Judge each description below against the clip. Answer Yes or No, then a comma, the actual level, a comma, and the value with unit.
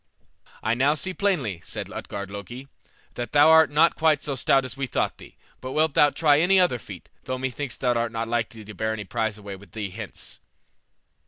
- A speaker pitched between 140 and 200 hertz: No, low, 125 Hz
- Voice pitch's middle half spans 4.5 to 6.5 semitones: Yes, average, 5.1 semitones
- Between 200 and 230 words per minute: Yes, fast, 205 wpm